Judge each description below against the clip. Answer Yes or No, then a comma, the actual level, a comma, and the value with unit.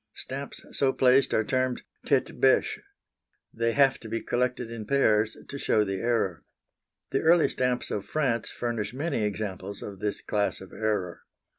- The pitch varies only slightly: No, average, 3.7 semitones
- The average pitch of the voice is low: Yes, low, 115 Hz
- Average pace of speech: Yes, average, 160 wpm